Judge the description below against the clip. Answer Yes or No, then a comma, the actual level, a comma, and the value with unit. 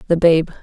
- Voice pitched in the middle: Yes, medium, 165 Hz